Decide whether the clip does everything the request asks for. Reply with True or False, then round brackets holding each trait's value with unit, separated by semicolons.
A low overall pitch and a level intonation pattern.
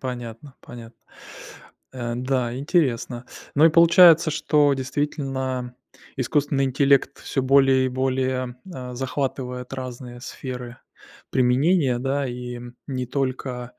True (130 Hz; 2.0 semitones)